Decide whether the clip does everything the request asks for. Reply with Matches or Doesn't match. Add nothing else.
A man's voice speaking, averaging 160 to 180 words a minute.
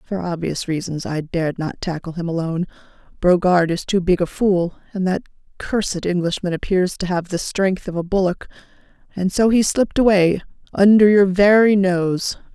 Doesn't match